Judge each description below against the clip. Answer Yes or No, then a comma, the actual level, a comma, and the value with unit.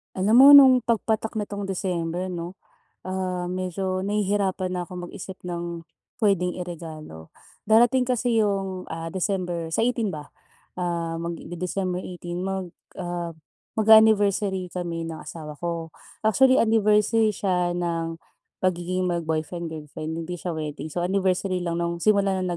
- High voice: No, medium, 180 Hz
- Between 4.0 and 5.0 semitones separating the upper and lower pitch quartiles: No, average, 2.9 semitones